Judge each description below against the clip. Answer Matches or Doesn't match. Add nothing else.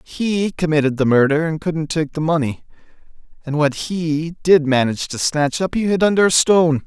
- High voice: Doesn't match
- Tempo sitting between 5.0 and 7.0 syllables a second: Matches